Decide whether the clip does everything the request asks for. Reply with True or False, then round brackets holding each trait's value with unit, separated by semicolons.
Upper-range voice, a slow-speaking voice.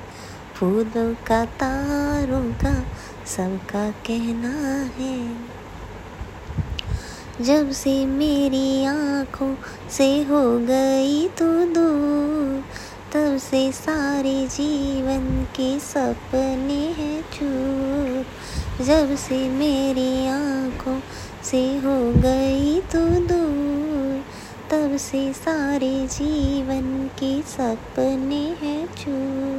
True (270 Hz; 80 wpm)